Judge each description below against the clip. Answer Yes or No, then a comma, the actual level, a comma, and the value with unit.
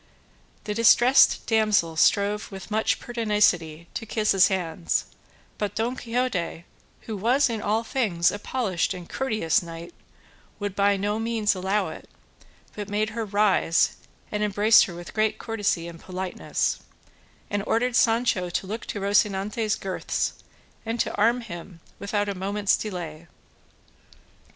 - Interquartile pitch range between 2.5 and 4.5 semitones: Yes, average, 3.1 semitones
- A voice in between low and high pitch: No, high, 205 Hz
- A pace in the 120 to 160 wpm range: Yes, average, 140 wpm